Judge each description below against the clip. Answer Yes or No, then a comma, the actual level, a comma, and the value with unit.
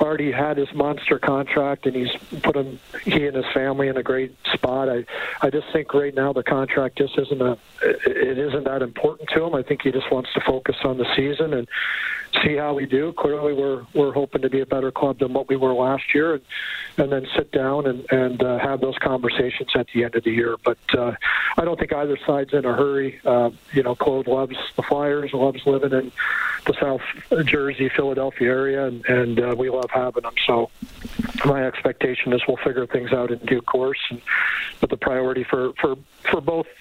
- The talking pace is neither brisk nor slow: No, fast, 215 wpm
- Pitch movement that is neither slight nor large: No, narrow, 2.0 semitones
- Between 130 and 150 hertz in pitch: Yes, low, 135 Hz